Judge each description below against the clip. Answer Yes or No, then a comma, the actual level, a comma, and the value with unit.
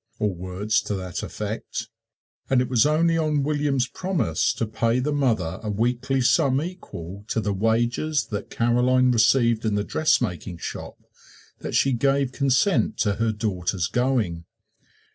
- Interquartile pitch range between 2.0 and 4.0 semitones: No, average, 4.7 semitones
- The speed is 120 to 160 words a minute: Yes, average, 150 wpm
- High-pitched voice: No, low, 115 Hz